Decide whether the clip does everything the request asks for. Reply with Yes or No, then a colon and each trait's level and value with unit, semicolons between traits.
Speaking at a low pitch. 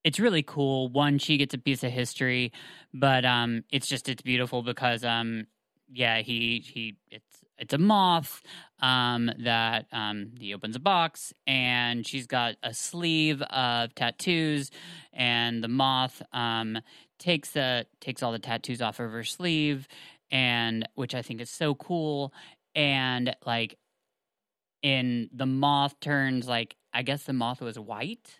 Yes: low, 125 Hz